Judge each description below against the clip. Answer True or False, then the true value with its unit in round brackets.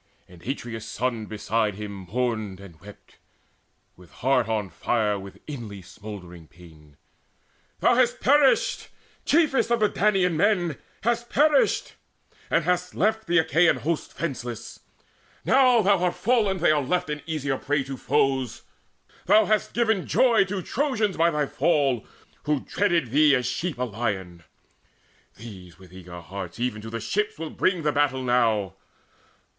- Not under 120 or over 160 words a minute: True (150 wpm)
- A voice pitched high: False (135 Hz)